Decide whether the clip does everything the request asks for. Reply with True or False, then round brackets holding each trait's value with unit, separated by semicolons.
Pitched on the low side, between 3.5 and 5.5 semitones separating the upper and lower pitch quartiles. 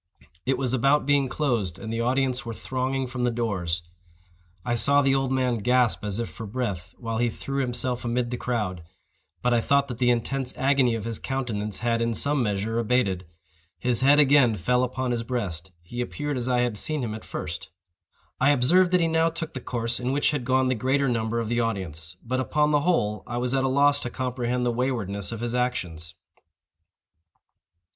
False (125 Hz; 2.8 semitones)